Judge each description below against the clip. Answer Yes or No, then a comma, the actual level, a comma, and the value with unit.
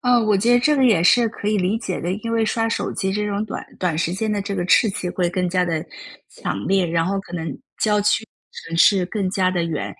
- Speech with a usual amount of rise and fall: Yes, average, 3.3 semitones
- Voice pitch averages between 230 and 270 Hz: No, high, 195 Hz